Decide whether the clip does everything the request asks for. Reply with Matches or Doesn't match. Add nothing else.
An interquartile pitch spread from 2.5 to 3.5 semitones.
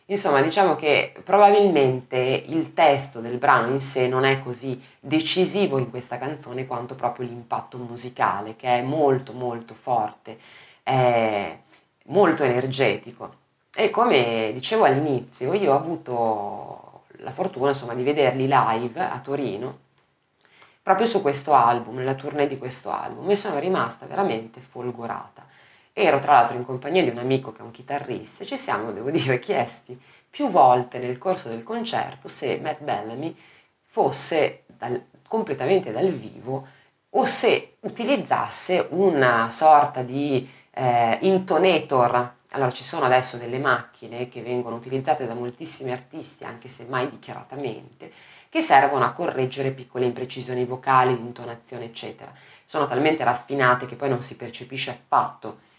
Matches